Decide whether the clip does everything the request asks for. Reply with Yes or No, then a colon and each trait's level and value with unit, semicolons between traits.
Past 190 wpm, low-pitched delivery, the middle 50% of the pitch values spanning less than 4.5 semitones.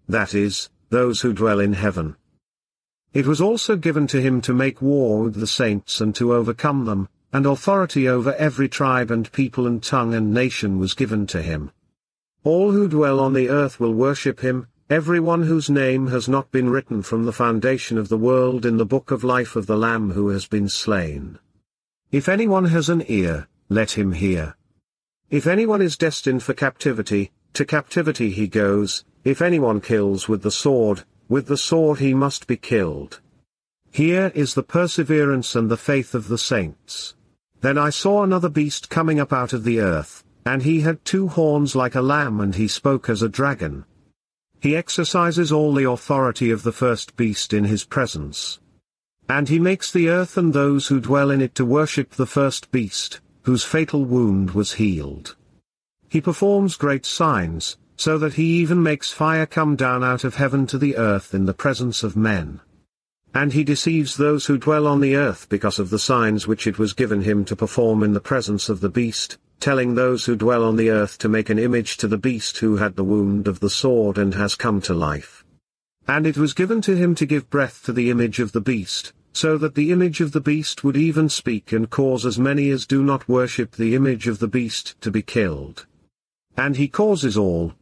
No: average, 200 wpm; low, 125 Hz; average, 5.2 semitones